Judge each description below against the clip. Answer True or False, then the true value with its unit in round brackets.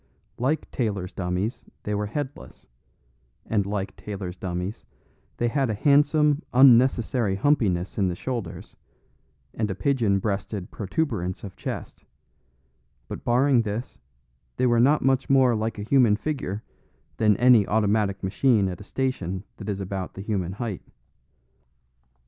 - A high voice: False (110 Hz)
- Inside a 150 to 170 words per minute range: False (135 wpm)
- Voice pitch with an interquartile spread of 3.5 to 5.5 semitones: True (4.7 semitones)